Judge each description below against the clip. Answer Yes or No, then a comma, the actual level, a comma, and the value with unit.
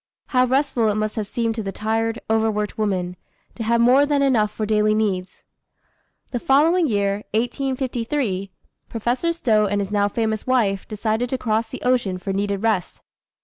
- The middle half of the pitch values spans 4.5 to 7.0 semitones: No, average, 3.3 semitones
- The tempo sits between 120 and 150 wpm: No, average, 175 wpm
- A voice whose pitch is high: Yes, high, 220 Hz